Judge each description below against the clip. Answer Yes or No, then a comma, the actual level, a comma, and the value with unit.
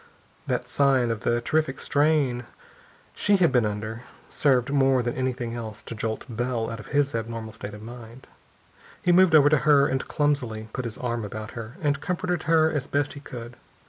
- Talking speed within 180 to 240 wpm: Yes, average, 190 wpm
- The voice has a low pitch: Yes, low, 125 Hz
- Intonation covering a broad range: No, average, 4.1 semitones